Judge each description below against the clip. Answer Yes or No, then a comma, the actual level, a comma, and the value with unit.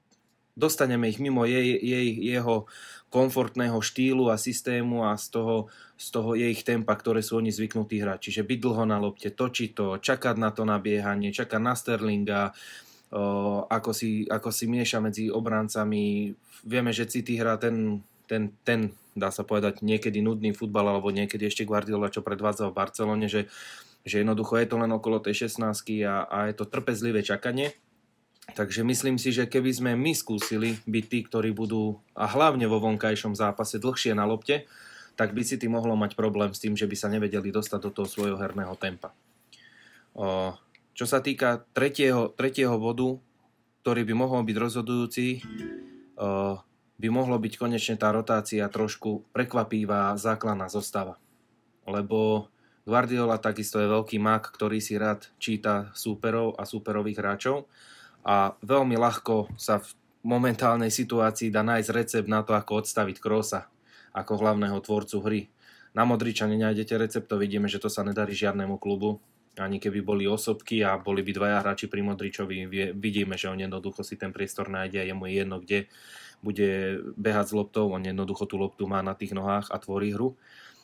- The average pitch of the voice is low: Yes, low, 110 Hz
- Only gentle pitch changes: Yes, narrow, 2.1 semitones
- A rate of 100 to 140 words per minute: No, fast, 165 wpm